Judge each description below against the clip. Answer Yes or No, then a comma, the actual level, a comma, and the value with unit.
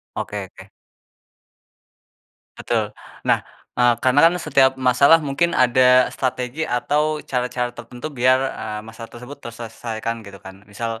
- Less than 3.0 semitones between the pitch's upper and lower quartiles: Yes, narrow, 2.4 semitones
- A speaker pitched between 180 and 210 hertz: No, low, 125 Hz